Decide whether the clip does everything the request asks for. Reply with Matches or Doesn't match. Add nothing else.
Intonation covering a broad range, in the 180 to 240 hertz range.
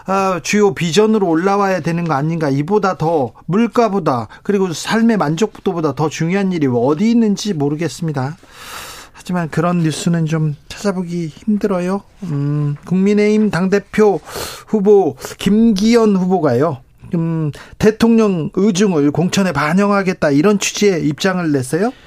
Doesn't match